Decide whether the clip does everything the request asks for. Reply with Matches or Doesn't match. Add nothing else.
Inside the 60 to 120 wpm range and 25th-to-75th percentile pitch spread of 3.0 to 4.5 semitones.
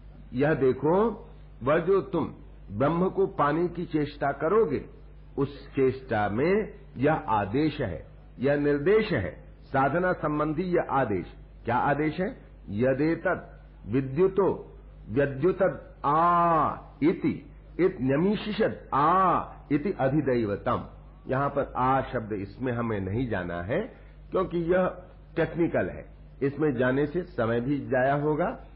Doesn't match